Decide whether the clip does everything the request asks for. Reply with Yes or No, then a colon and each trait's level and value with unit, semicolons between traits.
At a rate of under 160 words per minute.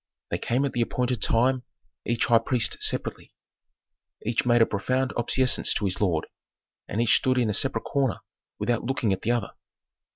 No: average, 175 wpm